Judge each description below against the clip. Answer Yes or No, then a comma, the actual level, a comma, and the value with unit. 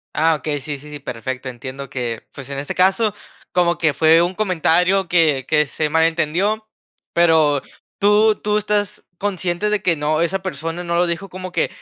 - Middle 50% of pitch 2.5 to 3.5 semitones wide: No, average, 4.2 semitones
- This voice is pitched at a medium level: Yes, medium, 165 Hz